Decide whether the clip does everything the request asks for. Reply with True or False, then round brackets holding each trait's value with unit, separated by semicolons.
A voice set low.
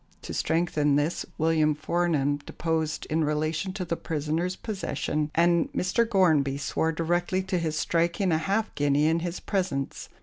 False (165 Hz)